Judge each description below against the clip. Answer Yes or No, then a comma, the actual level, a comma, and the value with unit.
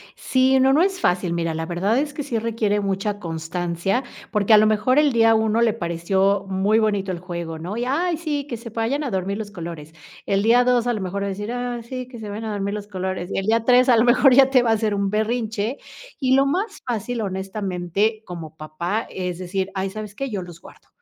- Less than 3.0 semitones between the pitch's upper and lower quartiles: No, average, 4.4 semitones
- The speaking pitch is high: Yes, high, 210 Hz